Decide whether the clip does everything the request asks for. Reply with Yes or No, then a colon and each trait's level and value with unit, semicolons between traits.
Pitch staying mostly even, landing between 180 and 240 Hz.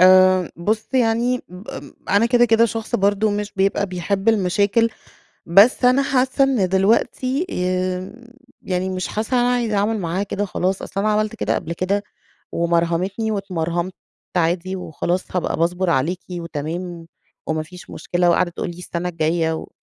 No: average, 3.7 semitones; medium, 185 Hz